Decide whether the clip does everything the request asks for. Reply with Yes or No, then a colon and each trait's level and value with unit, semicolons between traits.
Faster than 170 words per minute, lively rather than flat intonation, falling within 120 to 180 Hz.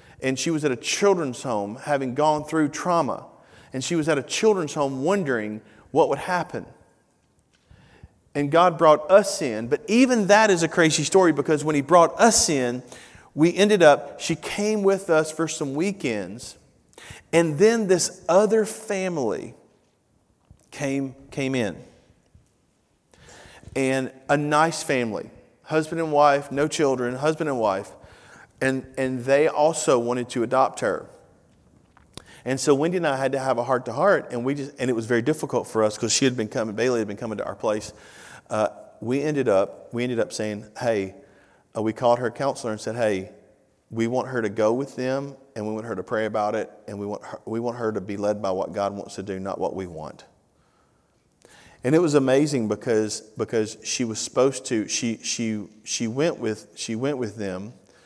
Yes: average, 185 wpm; wide, 6.0 semitones; low, 135 Hz